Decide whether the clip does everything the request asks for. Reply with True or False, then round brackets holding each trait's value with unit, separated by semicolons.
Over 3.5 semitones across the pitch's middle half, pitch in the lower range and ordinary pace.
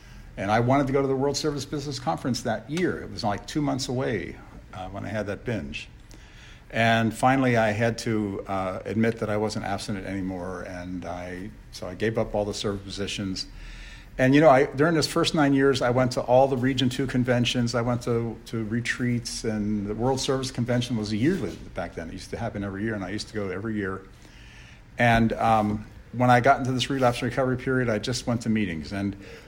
False (4.0 semitones; 115 Hz; 220 wpm)